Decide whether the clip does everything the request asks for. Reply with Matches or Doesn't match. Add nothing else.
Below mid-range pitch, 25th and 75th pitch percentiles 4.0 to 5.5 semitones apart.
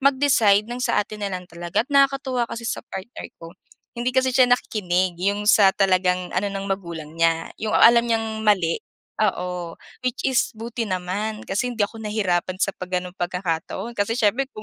Doesn't match